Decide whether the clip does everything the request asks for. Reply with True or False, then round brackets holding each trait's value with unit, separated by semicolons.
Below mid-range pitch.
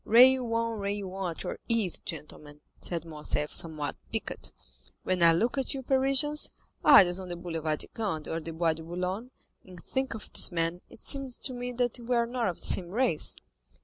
False (190 Hz)